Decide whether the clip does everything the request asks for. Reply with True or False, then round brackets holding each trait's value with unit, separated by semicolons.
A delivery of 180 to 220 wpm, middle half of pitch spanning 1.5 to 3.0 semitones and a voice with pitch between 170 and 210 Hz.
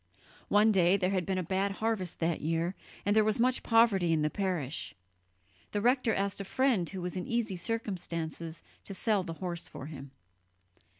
False (185 wpm; 4.0 semitones; 190 Hz)